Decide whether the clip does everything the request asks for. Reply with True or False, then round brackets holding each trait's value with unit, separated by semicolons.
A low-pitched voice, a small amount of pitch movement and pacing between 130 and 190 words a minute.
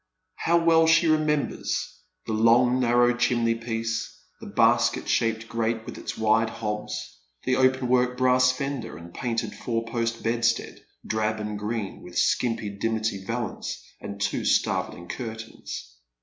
True (115 Hz; 2.3 semitones; 140 wpm)